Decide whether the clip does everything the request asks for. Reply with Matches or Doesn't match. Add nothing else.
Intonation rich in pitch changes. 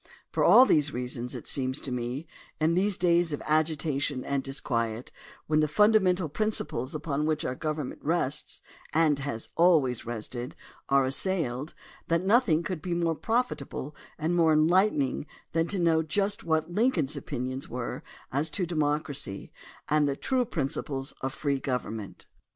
Doesn't match